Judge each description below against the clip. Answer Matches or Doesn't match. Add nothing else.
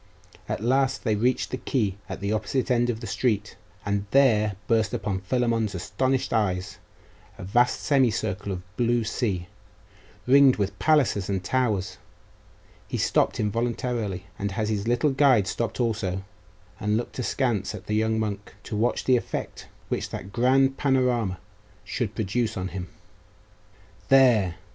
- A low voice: Matches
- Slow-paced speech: Doesn't match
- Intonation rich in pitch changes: Doesn't match